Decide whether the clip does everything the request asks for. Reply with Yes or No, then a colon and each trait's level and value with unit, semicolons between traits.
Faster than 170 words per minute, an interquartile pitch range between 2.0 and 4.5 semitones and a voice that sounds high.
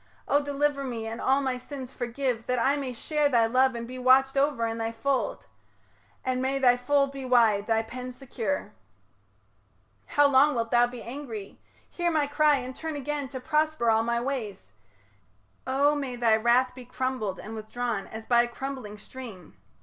Yes: average, 180 wpm; average, 3.1 semitones; very high, 255 Hz